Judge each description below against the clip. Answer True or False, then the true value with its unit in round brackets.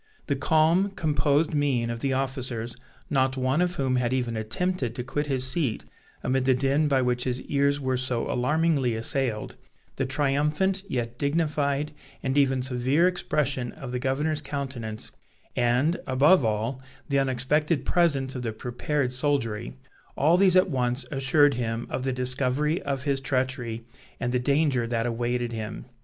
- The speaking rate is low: False (160 wpm)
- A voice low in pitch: True (130 Hz)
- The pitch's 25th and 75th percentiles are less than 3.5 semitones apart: True (2.9 semitones)